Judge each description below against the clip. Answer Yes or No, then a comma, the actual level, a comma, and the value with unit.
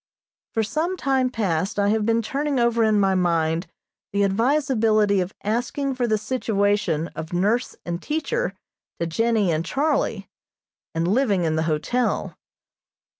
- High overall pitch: Yes, high, 215 Hz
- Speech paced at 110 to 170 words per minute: Yes, average, 145 wpm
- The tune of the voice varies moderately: No, wide, 5.7 semitones